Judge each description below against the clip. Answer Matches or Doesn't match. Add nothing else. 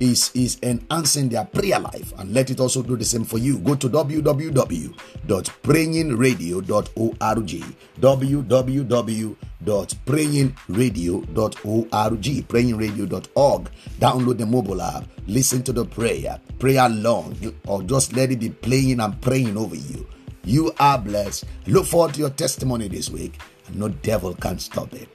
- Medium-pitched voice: Doesn't match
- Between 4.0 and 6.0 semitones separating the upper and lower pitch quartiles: Doesn't match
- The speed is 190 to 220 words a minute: Doesn't match